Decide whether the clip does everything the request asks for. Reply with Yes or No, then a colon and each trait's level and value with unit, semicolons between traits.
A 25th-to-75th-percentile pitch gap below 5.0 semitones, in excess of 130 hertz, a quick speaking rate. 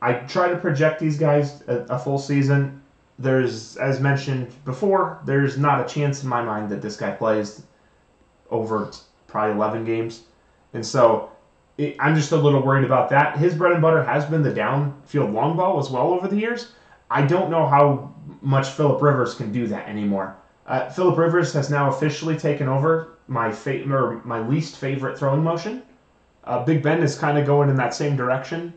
No: average, 3.9 semitones; medium, 140 Hz; average, 190 wpm